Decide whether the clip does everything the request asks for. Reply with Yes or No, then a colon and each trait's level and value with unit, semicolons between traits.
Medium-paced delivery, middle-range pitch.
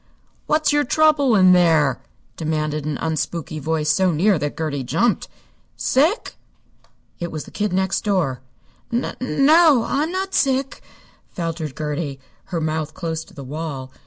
Yes: average, 145 wpm; medium, 170 Hz